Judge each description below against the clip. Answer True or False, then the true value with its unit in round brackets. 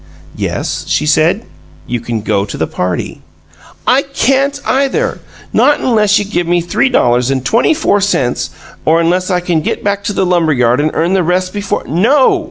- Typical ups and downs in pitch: False (6.5 semitones)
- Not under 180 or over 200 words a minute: True (190 wpm)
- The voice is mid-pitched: True (180 Hz)